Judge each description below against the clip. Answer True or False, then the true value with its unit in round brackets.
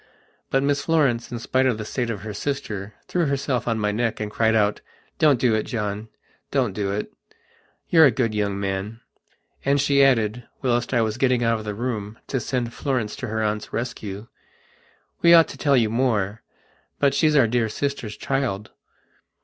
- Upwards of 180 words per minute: True (190 wpm)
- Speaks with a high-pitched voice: False (115 Hz)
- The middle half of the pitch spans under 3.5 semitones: False (4.0 semitones)